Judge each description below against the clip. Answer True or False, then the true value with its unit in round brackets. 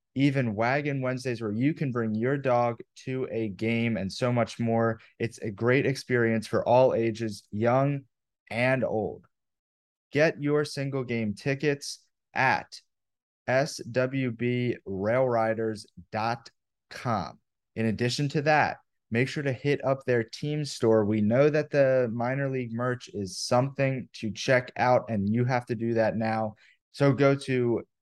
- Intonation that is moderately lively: True (3.2 semitones)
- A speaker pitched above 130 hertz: False (125 Hz)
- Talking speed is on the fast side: False (145 wpm)